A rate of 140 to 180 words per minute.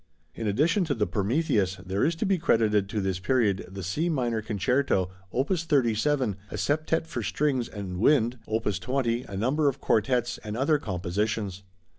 Yes: average, 170 wpm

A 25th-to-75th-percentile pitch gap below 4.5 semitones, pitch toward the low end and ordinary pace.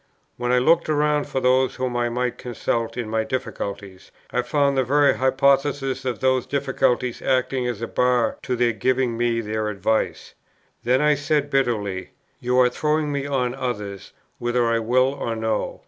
Yes: average, 2.7 semitones; low, 125 Hz; average, 175 wpm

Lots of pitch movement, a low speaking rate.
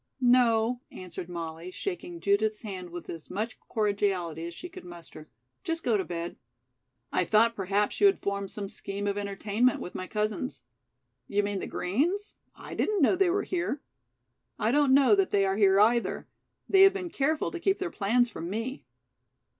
No: wide, 6.9 semitones; average, 180 wpm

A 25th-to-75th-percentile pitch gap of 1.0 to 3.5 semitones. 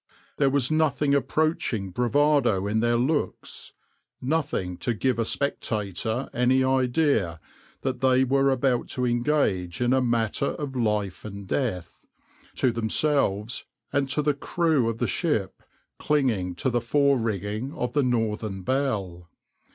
No: average, 4.6 semitones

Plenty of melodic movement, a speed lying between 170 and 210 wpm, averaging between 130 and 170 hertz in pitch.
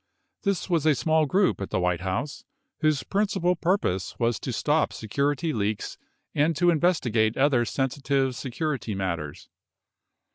No: wide, 6.5 semitones; average, 140 wpm; medium, 140 Hz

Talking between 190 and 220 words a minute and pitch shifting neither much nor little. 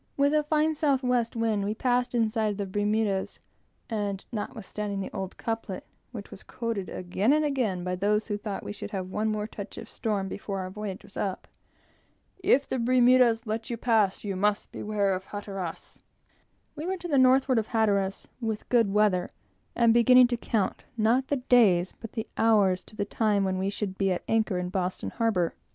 Yes: average, 200 wpm; average, 3.4 semitones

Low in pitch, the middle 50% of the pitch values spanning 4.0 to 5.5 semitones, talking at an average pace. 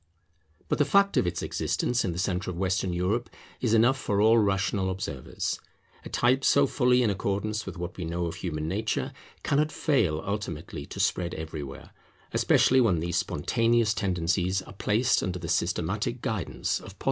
Yes: very low, 95 Hz; average, 5.0 semitones; average, 175 wpm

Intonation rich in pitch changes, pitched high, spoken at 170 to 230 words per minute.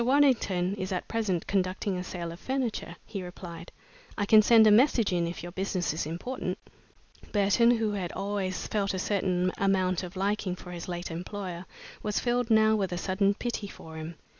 No: average, 3.2 semitones; high, 195 Hz; average, 190 wpm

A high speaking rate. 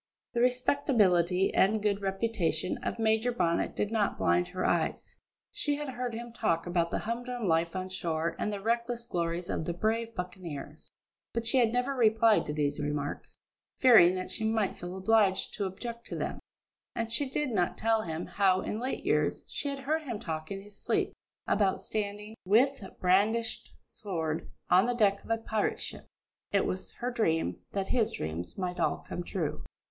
No: average, 185 wpm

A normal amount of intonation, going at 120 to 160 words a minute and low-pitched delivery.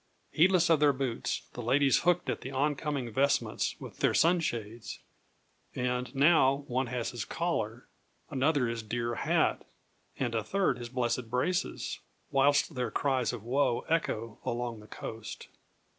Yes: average, 3.3 semitones; average, 145 wpm; low, 130 Hz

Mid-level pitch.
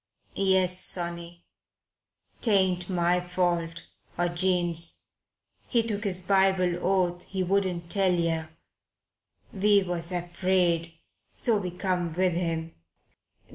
Yes: medium, 180 Hz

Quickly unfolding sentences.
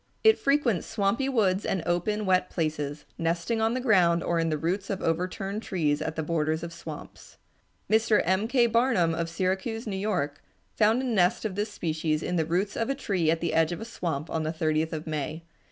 Yes: fast, 210 wpm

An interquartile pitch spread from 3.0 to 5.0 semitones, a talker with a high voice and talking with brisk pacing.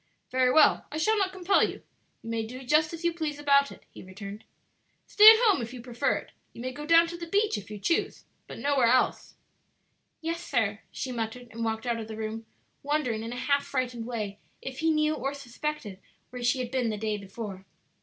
No: wide, 5.4 semitones; very high, 255 Hz; fast, 220 wpm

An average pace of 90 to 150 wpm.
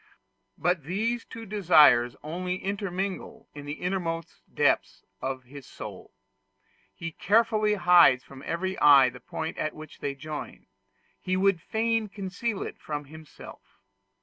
Yes: slow, 135 wpm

